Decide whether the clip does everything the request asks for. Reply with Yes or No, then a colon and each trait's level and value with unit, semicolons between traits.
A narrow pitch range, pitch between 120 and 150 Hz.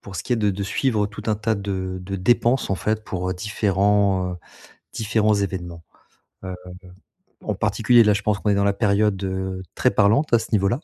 No: narrow, 2.3 semitones; low, 100 Hz